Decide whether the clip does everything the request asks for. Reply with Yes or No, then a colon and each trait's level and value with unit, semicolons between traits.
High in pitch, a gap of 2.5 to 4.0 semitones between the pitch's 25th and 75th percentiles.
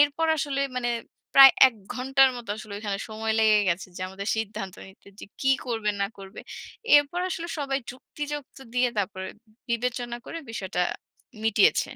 No: high, 235 Hz; average, 4.9 semitones